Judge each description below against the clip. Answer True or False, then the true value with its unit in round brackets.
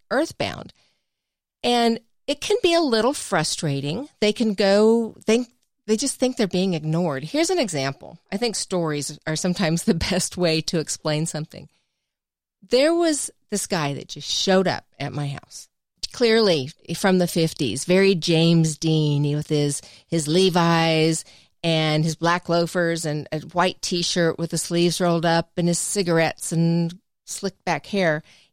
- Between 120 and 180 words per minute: True (160 wpm)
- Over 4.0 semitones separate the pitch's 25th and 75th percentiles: True (4.5 semitones)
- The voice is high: False (170 Hz)